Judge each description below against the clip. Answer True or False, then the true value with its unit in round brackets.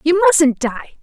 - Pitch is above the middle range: True (310 Hz)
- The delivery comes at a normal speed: True (175 wpm)